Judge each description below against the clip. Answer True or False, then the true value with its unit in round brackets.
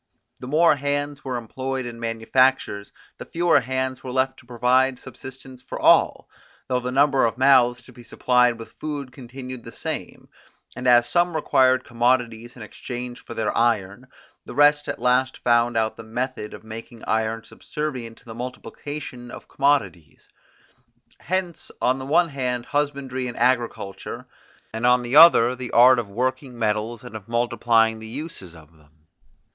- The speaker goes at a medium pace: True (165 wpm)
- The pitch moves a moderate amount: False (2.3 semitones)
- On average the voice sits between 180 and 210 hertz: False (125 Hz)